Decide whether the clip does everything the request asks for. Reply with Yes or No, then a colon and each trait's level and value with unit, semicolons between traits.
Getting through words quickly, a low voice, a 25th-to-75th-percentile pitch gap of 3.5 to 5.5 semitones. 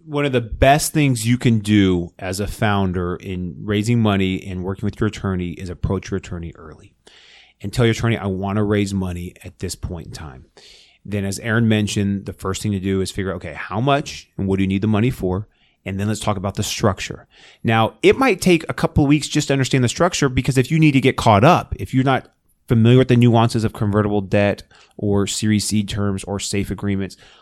Yes: fast, 230 wpm; low, 105 Hz; average, 3.8 semitones